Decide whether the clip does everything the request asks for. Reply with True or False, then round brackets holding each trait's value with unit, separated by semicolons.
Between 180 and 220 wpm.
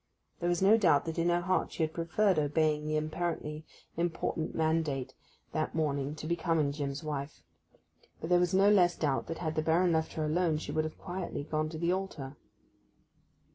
True (190 wpm)